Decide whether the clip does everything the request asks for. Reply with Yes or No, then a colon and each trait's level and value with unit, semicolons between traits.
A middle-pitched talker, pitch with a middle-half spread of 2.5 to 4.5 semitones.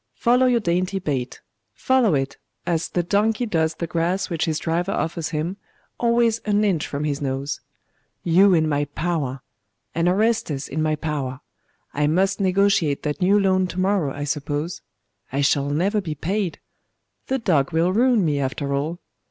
No: medium, 170 Hz; average, 5.1 semitones